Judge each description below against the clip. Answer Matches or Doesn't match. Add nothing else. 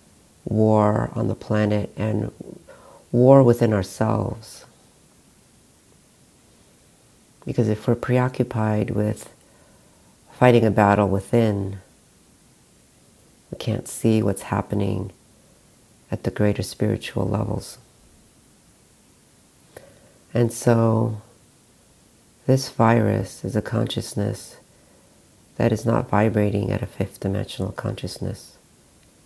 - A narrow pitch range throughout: Matches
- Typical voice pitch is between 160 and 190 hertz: Doesn't match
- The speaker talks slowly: Matches